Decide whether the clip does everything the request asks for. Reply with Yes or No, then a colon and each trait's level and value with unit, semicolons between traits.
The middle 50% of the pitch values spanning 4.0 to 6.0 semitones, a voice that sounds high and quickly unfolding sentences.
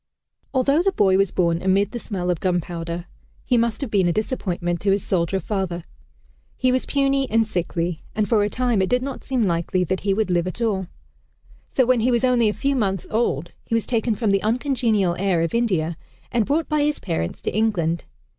Yes: average, 5.2 semitones; high, 205 Hz; fast, 210 wpm